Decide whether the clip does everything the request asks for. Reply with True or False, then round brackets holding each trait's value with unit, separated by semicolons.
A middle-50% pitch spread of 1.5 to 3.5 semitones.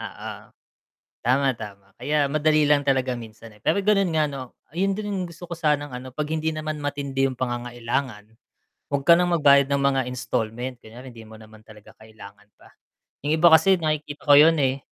False (4.1 semitones)